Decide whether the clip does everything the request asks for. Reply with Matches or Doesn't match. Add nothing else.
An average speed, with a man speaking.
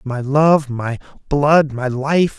Matches